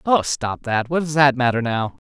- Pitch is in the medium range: No, low, 130 Hz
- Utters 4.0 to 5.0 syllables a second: Yes, 4.8 syllables/s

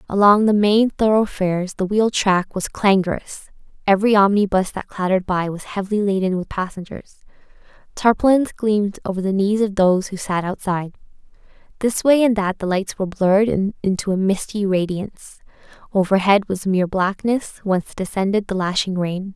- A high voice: Yes, high, 195 Hz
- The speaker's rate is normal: Yes, average, 155 wpm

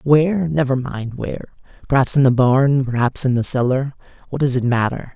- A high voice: No, low, 135 Hz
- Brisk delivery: No, average, 185 wpm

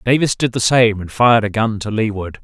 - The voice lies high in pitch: No, low, 110 Hz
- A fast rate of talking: Yes, fast, 245 wpm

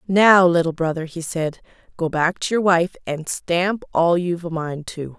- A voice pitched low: No, medium, 170 Hz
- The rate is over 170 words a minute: Yes, average, 195 wpm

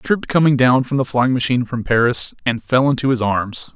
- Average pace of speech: No, fast, 210 wpm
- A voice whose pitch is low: Yes, low, 125 Hz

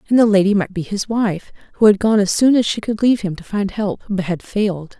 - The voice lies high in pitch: Yes, high, 205 Hz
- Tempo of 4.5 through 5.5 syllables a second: No, 5.8 syllables/s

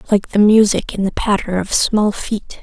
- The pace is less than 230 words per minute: Yes, fast, 205 wpm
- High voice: Yes, high, 205 Hz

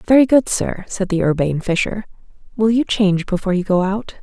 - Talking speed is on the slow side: No, average, 200 wpm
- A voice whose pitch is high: Yes, high, 200 Hz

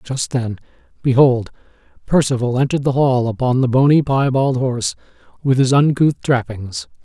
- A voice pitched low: Yes, low, 130 Hz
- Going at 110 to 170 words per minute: Yes, slow, 135 wpm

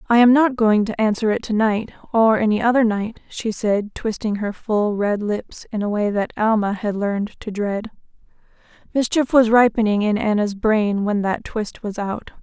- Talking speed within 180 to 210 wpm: Yes, average, 190 wpm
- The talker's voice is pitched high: Yes, high, 215 Hz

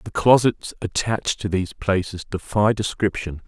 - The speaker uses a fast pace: No, average, 140 wpm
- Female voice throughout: No, male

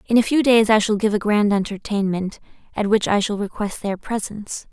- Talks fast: Yes, fast, 215 wpm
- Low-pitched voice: No, high, 210 Hz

